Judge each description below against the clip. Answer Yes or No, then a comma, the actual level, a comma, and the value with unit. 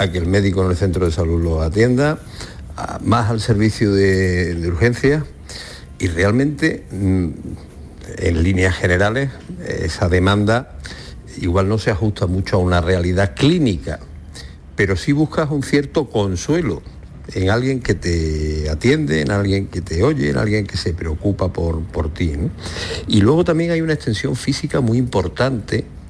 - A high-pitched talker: No, low, 100 Hz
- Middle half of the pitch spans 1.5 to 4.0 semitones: No, average, 5.0 semitones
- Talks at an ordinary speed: Yes, average, 155 wpm